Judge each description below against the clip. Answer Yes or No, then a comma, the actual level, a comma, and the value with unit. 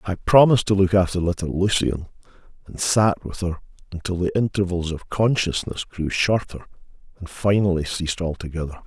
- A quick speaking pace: No, average, 150 wpm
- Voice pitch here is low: Yes, very low, 90 Hz